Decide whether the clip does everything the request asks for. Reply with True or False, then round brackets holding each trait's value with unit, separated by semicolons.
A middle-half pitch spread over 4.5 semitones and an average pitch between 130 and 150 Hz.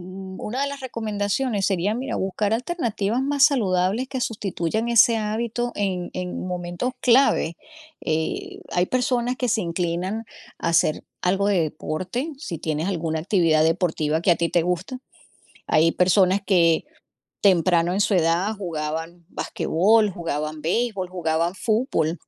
False (5.2 semitones; 185 Hz)